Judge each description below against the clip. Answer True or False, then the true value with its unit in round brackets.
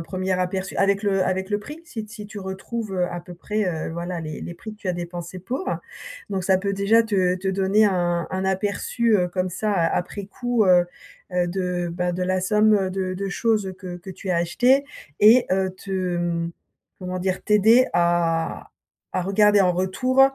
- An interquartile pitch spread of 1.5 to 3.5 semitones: True (2.7 semitones)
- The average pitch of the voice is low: False (190 Hz)